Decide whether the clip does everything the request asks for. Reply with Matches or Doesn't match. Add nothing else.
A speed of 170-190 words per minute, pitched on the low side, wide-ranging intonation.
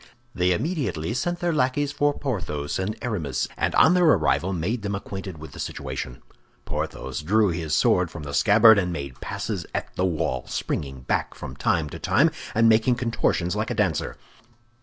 Matches